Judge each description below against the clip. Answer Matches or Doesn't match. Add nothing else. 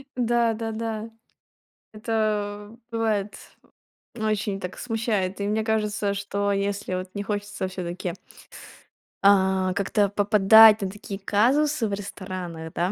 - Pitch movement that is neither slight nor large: Doesn't match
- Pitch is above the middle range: Matches